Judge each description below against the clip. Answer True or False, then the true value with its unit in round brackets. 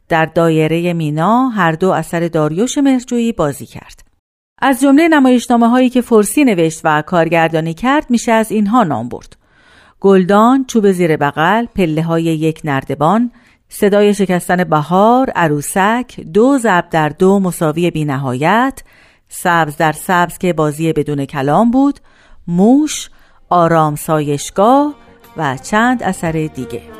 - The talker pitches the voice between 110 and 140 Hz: False (180 Hz)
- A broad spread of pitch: True (6.7 semitones)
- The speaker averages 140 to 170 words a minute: False (130 wpm)